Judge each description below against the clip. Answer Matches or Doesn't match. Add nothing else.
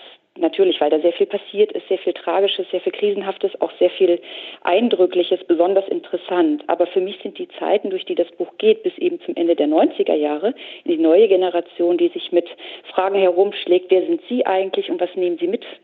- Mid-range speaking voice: Doesn't match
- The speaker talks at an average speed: Doesn't match